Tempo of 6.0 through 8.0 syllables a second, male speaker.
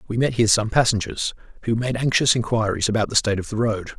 Yes: 6.7 syllables/s; male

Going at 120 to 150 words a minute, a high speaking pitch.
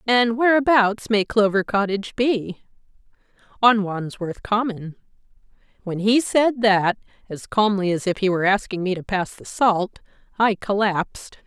Yes: average, 140 wpm; high, 205 Hz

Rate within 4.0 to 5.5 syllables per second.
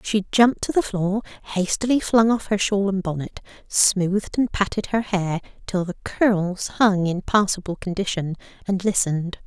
Yes: 4.7 syllables/s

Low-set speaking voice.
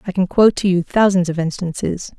No: medium, 185 Hz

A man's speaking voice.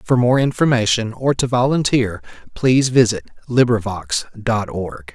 Yes: male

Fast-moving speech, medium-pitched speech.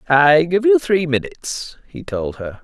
No: average, 180 wpm; medium, 160 Hz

